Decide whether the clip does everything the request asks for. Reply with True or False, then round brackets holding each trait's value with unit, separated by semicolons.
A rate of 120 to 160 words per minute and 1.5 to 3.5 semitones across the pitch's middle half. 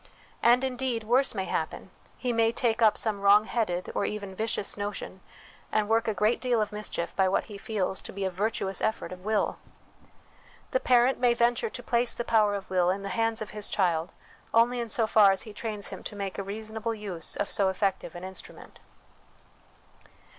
False (200 wpm; 2.8 semitones)